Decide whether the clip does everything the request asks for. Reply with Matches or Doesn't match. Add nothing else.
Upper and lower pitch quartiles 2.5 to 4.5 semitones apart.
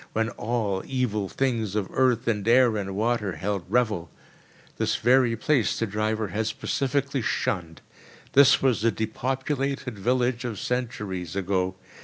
Matches